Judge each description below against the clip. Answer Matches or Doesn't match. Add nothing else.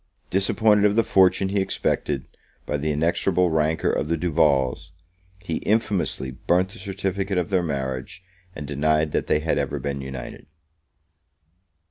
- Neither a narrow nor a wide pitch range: Matches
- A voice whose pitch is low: Matches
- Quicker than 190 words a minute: Doesn't match